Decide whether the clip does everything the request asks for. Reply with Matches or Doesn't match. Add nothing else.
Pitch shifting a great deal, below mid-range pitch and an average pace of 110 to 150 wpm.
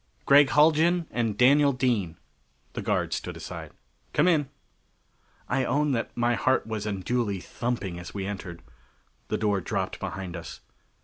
Matches